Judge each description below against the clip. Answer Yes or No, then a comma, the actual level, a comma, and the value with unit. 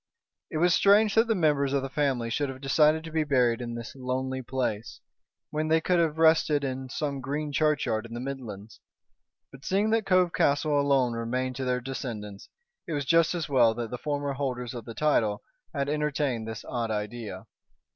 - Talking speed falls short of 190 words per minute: No, average, 195 wpm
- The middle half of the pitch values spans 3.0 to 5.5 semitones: Yes, average, 4.2 semitones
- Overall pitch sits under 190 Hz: Yes, low, 135 Hz